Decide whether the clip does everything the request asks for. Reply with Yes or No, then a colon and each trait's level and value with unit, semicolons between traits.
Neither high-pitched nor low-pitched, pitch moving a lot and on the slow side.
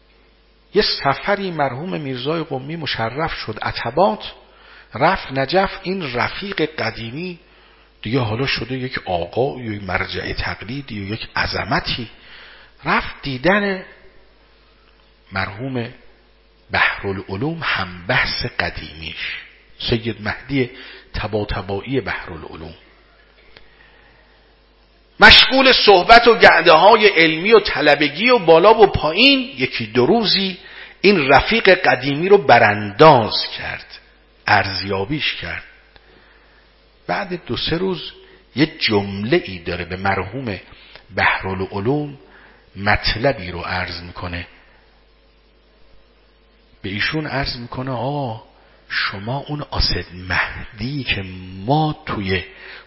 No: low, 130 Hz; wide, 8.4 semitones; slow, 100 wpm